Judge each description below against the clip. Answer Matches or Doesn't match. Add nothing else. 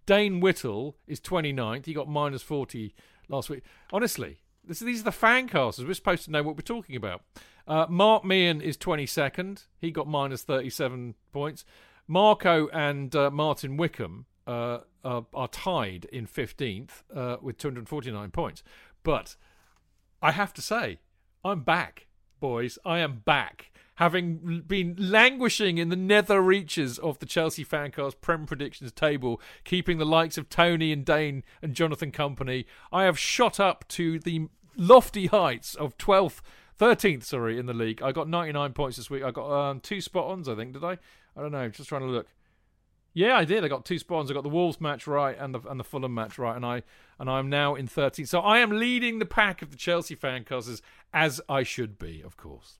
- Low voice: Doesn't match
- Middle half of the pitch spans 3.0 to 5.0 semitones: Doesn't match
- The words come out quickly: Doesn't match